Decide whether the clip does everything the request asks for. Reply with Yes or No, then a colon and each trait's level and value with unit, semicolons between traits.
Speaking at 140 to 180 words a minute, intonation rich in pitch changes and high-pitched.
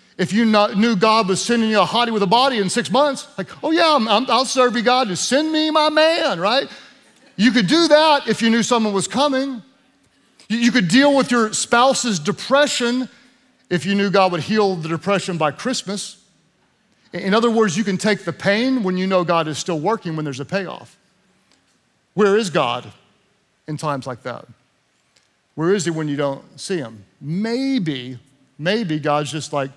No: average, 195 wpm; wide, 6.0 semitones; high, 210 Hz